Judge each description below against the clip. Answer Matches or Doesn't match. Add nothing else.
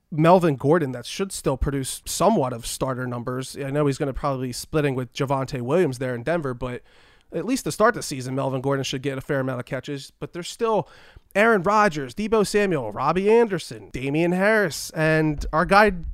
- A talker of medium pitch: Matches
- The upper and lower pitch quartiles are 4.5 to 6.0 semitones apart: Matches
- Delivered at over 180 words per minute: Matches